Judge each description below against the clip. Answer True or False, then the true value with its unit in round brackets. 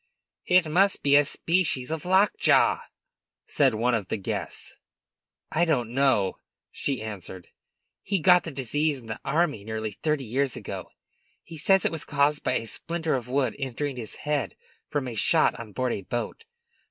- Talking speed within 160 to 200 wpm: True (170 wpm)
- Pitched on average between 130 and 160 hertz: True (140 Hz)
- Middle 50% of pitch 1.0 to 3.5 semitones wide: False (5.4 semitones)